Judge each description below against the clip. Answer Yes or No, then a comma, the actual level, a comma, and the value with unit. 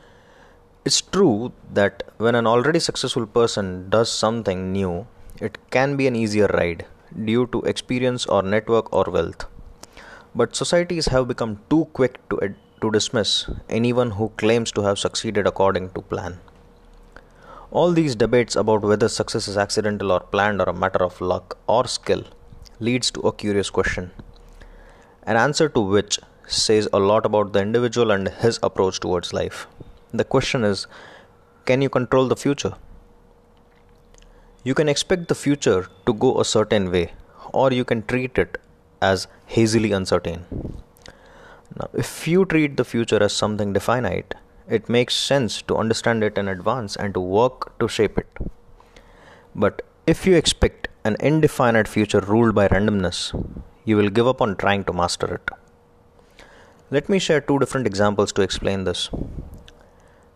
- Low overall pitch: Yes, low, 110 Hz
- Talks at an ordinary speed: Yes, average, 155 wpm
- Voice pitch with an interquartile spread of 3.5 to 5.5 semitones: Yes, average, 4.4 semitones